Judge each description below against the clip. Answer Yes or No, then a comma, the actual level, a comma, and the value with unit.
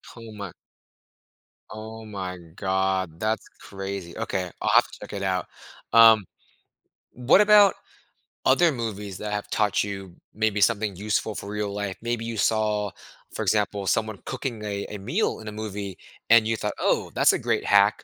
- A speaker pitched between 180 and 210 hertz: No, low, 105 Hz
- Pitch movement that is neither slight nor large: No, narrow, 2.1 semitones